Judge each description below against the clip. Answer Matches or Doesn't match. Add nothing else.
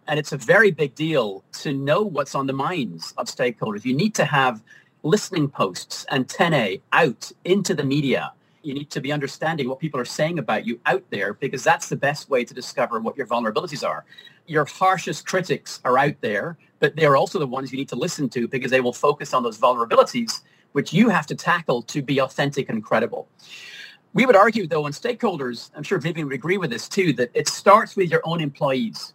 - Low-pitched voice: Doesn't match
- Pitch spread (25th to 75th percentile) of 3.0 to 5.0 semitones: Doesn't match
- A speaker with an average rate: Doesn't match